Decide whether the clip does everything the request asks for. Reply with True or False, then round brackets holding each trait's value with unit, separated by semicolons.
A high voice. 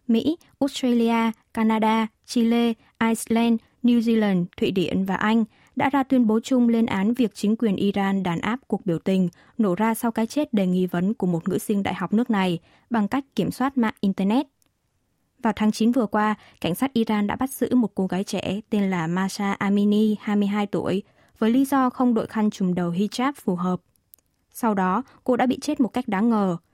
True (220 Hz)